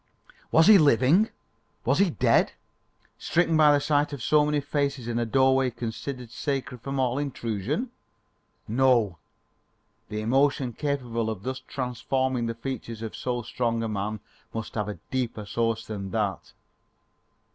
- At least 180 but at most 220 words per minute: No, average, 145 wpm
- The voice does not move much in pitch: No, average, 3.8 semitones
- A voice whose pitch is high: No, low, 125 Hz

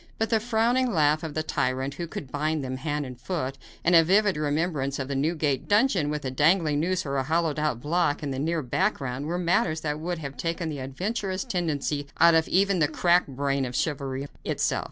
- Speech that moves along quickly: Yes, fast, 215 wpm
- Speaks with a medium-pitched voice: Yes, medium, 155 Hz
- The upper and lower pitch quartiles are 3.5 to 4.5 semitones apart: Yes, average, 3.9 semitones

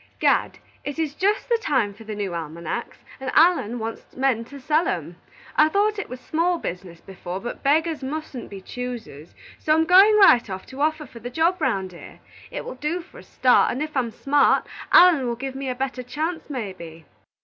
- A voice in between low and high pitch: No, very high, 265 Hz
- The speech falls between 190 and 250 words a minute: Yes, fast, 205 wpm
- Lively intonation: Yes, wide, 6.2 semitones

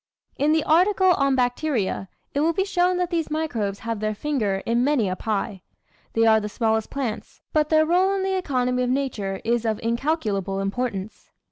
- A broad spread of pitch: Yes, wide, 6.5 semitones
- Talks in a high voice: Yes, very high, 250 Hz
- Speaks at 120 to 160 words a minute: No, average, 190 wpm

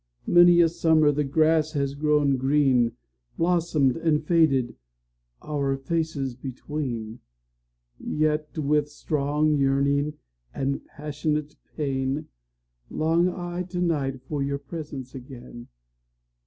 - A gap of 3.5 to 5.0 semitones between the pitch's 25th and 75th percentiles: No, average, 2.8 semitones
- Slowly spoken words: Yes, slow, 95 wpm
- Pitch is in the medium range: Yes, medium, 145 Hz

